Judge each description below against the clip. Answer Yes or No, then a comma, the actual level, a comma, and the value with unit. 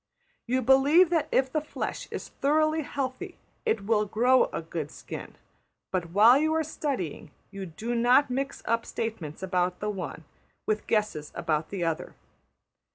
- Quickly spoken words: No, average, 160 wpm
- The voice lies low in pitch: No, high, 230 Hz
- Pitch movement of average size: No, wide, 6.9 semitones